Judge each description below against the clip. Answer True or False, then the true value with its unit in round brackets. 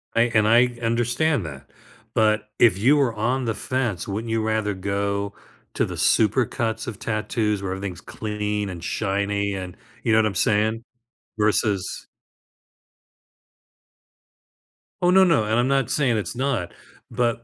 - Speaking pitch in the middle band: False (110 Hz)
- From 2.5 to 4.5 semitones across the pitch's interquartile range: True (2.9 semitones)